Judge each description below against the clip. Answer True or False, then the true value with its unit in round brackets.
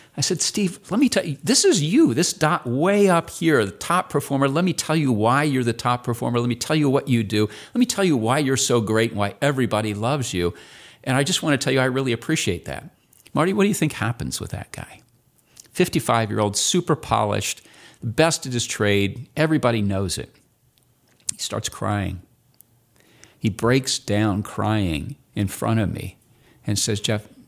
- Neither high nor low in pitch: False (125 Hz)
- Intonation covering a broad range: True (6.3 semitones)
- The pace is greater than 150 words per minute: True (200 wpm)